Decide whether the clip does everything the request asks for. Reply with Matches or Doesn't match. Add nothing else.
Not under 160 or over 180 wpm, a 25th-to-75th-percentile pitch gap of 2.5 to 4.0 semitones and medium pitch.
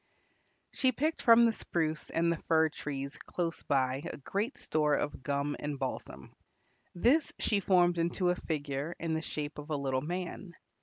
Matches